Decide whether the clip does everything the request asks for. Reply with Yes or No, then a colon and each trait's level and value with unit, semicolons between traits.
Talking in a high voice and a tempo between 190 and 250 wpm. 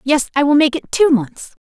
No: very high, 280 Hz; fast, 260 wpm